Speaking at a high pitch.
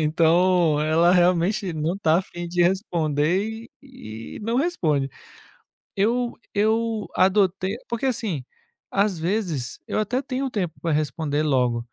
No: medium, 180 Hz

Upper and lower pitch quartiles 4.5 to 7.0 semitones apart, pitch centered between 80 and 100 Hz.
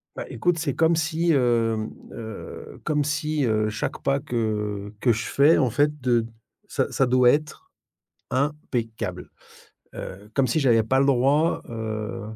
No: average, 5.0 semitones; low, 125 Hz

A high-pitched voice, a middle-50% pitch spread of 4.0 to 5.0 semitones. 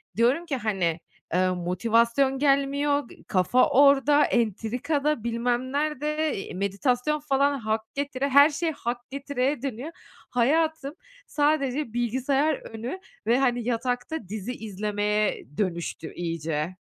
Yes: very high, 250 Hz; average, 4.6 semitones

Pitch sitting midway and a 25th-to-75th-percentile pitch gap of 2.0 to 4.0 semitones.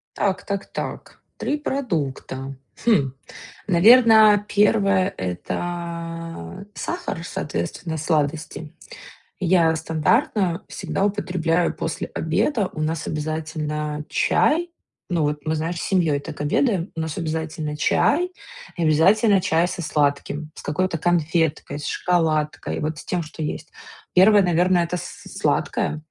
Yes: medium, 165 Hz; average, 3.6 semitones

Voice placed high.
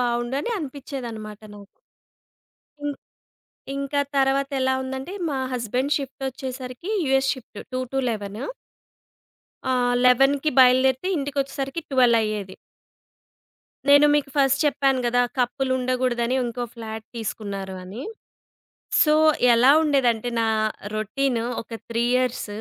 Yes: very high, 255 Hz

